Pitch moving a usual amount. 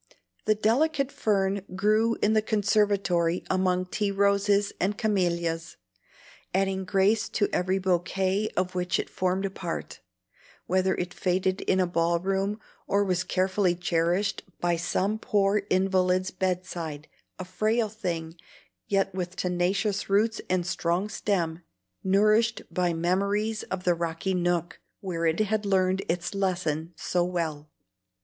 No: narrow, 2.3 semitones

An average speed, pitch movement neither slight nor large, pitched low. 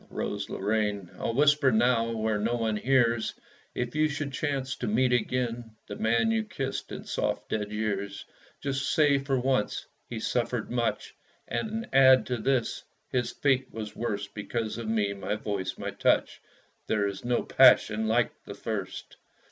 Yes: average, 165 wpm; average, 3.5 semitones; low, 120 Hz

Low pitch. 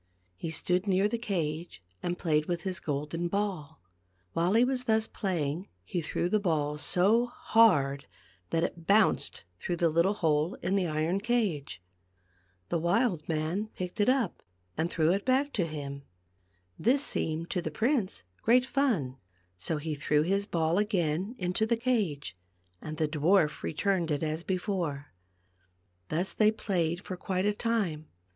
No: medium, 175 Hz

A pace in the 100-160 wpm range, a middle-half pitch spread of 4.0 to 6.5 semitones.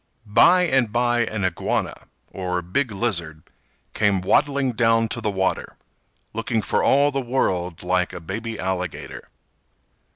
Yes: slow, 135 wpm; average, 4.6 semitones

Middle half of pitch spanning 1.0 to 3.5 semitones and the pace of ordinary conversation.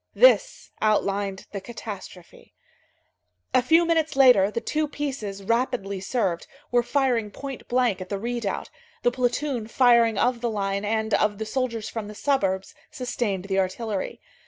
No: average, 4.1 semitones; average, 150 wpm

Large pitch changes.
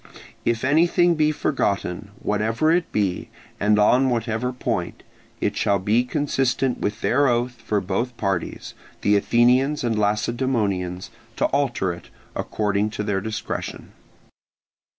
No: average, 4.1 semitones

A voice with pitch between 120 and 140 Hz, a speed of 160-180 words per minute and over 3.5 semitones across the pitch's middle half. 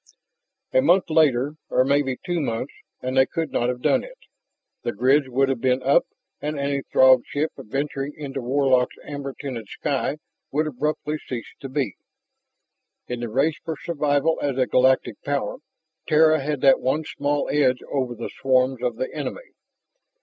No: low, 135 Hz; average, 165 wpm; narrow, 2.6 semitones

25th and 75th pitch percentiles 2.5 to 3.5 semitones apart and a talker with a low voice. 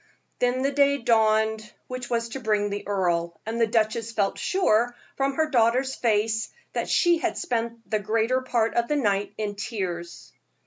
No: average, 3.1 semitones; high, 225 Hz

